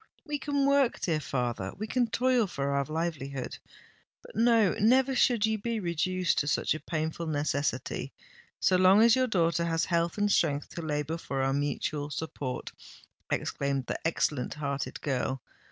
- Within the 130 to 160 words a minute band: Yes, average, 155 wpm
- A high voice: No, medium, 165 Hz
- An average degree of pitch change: No, wide, 7.3 semitones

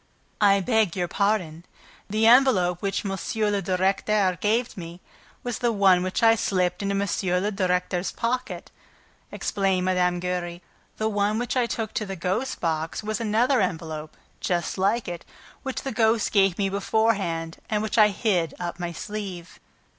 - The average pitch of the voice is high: Yes, high, 195 Hz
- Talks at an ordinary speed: Yes, average, 160 wpm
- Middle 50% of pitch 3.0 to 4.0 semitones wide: Yes, average, 3.4 semitones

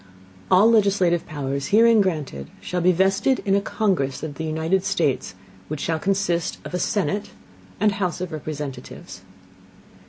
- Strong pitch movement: No, average, 4.4 semitones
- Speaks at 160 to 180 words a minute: No, average, 150 wpm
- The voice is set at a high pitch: No, medium, 180 Hz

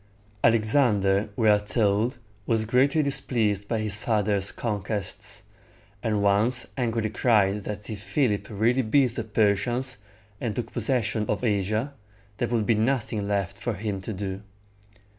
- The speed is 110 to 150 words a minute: Yes, average, 140 wpm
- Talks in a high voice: No, low, 110 Hz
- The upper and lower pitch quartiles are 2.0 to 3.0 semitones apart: Yes, average, 2.7 semitones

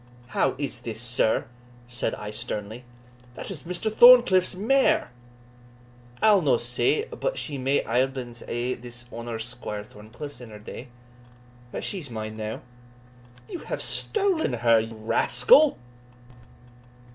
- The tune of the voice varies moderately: No, wide, 8.1 semitones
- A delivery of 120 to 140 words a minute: Yes, slow, 135 wpm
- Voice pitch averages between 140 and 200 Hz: No, low, 125 Hz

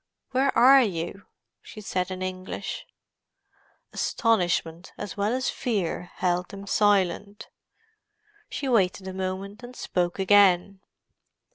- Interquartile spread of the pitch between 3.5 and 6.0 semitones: No, average, 2.9 semitones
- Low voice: No, high, 195 Hz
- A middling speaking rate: No, slow, 115 wpm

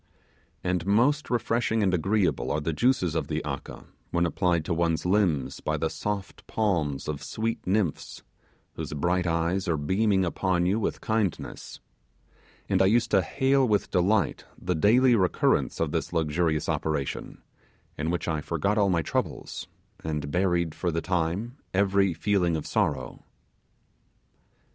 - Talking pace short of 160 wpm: Yes, average, 150 wpm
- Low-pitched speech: Yes, very low, 90 Hz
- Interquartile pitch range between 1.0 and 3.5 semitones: No, average, 4.2 semitones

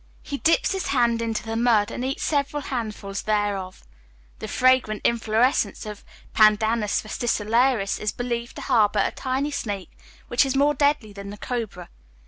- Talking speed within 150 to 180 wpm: Yes, average, 155 wpm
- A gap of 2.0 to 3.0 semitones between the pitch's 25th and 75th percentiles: No, average, 3.7 semitones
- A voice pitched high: Yes, high, 230 Hz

